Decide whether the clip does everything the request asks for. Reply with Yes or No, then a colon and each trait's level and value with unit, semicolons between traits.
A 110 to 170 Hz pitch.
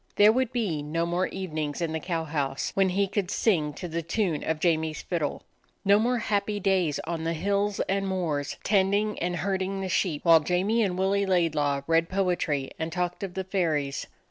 No: medium, 180 Hz